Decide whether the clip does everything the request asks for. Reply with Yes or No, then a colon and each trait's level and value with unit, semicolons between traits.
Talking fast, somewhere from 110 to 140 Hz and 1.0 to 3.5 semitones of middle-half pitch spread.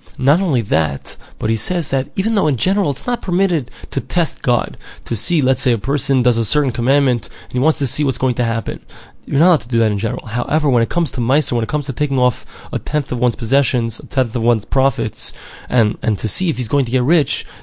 No: fast, 260 wpm; low, 130 Hz; average, 4.0 semitones